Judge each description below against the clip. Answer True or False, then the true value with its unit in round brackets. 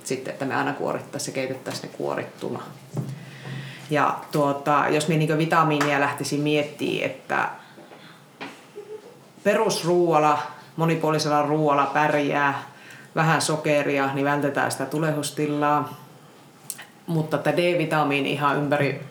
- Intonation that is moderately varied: False (1.6 semitones)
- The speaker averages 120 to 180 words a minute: False (105 wpm)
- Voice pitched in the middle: True (150 Hz)